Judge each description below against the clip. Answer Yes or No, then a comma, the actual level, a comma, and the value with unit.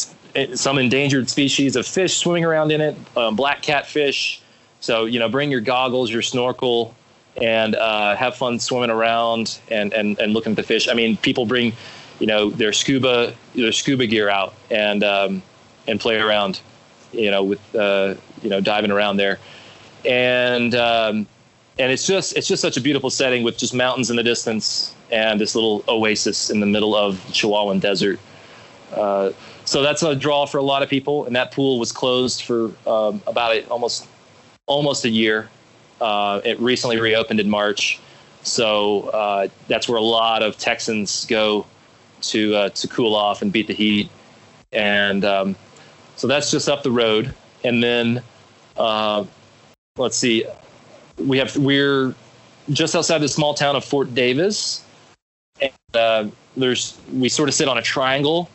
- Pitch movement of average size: Yes, average, 4.0 semitones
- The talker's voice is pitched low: Yes, low, 120 Hz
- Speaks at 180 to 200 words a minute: No, average, 170 wpm